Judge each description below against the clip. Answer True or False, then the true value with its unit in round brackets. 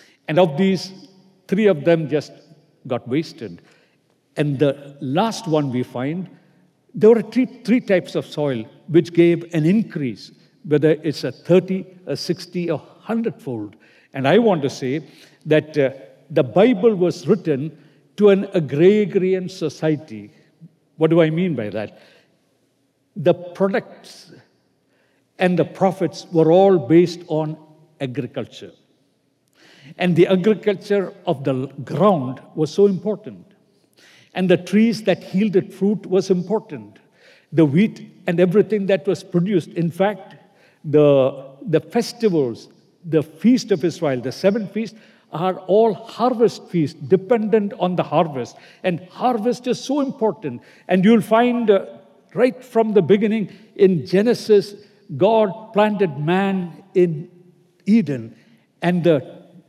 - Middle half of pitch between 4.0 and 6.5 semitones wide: True (4.4 semitones)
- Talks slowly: True (130 wpm)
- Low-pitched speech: False (180 Hz)